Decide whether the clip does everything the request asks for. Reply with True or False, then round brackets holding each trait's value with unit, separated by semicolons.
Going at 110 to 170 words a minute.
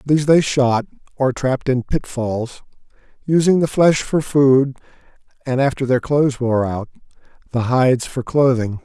True (150 wpm)